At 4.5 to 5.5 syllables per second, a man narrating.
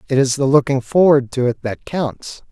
Yes: 4.9 syllables/s; male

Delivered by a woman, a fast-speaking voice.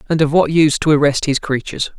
No: male; fast, 240 wpm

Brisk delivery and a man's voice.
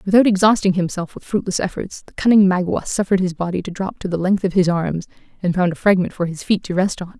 No: fast, 250 wpm; female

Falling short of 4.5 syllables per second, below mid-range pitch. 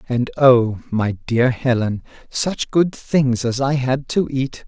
Yes: 3.4 syllables/s; low, 130 Hz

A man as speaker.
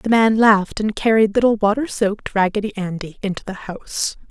No: female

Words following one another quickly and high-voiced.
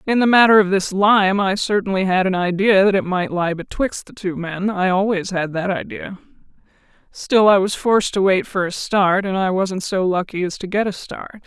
Yes: fast, 225 wpm; high, 195 Hz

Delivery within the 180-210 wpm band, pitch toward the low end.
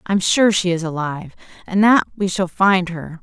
No: fast, 205 wpm; medium, 185 Hz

